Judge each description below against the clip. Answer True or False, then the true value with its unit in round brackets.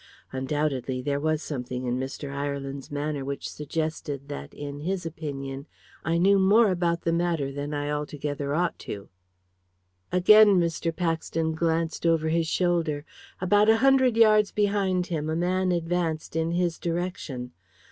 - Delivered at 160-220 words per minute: False (145 wpm)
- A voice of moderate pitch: True (160 Hz)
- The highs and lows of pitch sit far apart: False (3.7 semitones)